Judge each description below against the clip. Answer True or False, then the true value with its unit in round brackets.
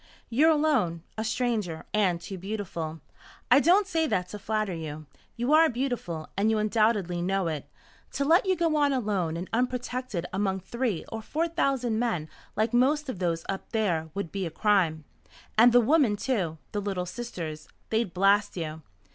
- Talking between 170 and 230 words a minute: True (175 wpm)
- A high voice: True (210 Hz)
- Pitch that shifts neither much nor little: False (6.0 semitones)